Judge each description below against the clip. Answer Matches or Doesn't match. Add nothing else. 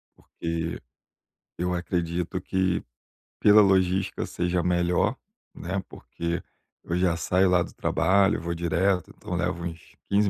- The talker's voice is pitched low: Matches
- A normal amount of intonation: Doesn't match